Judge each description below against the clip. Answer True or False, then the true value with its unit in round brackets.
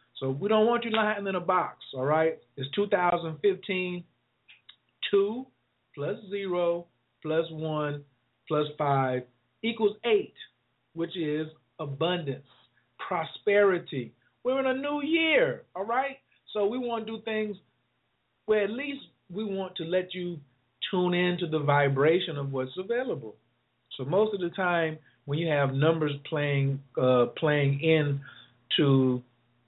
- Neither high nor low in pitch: True (165 Hz)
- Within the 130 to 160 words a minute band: True (140 wpm)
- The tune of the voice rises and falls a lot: True (6.2 semitones)